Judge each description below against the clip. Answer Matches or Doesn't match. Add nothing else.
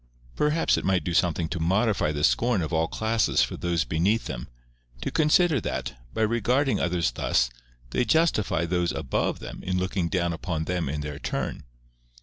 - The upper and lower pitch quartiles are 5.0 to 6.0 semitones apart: Matches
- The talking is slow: Doesn't match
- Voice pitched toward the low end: Matches